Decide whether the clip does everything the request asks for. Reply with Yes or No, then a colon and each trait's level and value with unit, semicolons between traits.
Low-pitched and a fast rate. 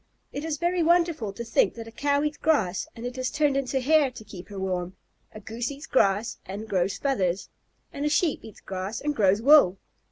No: high, 235 Hz; fast, 215 wpm